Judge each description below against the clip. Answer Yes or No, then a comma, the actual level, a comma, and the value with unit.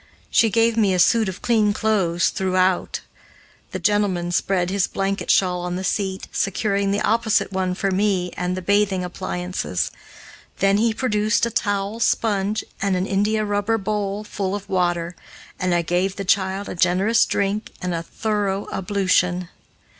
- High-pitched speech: Yes, high, 195 Hz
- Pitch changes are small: Yes, narrow, 2.2 semitones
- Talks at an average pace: Yes, average, 160 wpm